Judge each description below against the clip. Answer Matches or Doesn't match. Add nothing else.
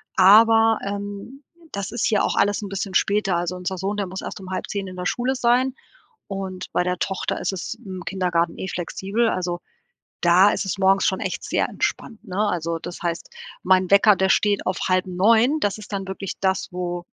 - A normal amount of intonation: Doesn't match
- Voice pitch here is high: Matches